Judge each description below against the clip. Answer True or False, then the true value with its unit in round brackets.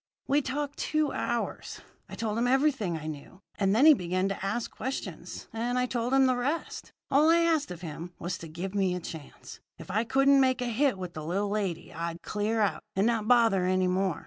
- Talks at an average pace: False (220 wpm)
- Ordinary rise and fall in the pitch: False (6.1 semitones)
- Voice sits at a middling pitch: False (215 Hz)